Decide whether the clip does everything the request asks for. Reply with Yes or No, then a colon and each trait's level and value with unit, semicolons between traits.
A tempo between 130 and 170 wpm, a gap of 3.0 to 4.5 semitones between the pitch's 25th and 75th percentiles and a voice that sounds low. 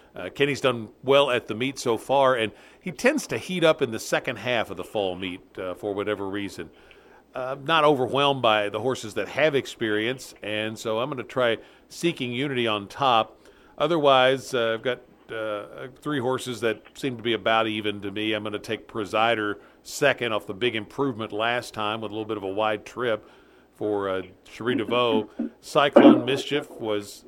No: average, 195 wpm; average, 4.2 semitones; low, 115 Hz